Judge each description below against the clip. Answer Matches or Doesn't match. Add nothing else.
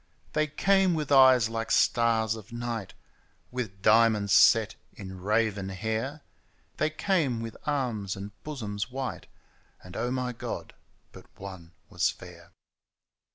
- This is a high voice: Doesn't match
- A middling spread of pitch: Matches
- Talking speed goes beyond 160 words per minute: Doesn't match